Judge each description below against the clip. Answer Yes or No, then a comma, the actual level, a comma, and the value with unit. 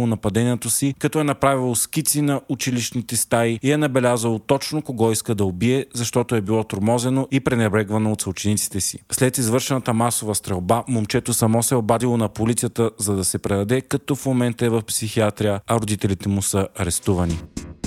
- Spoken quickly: Yes, fast, 175 wpm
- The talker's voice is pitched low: Yes, low, 115 Hz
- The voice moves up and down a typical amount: Yes, average, 3.2 semitones